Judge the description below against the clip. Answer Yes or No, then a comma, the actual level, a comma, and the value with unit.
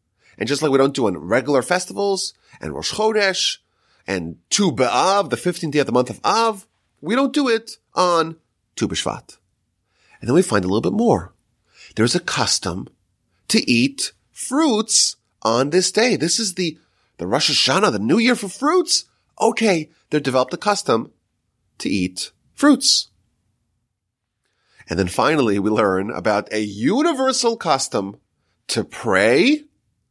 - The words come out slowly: No, average, 155 wpm